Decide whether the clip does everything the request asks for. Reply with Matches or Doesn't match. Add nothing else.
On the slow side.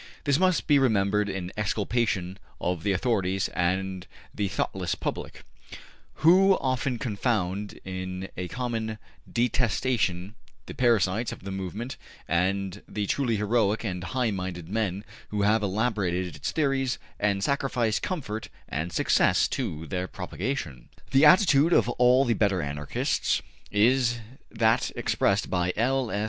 Matches